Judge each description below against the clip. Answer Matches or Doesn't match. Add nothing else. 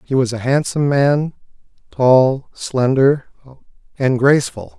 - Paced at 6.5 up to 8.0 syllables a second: Doesn't match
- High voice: Doesn't match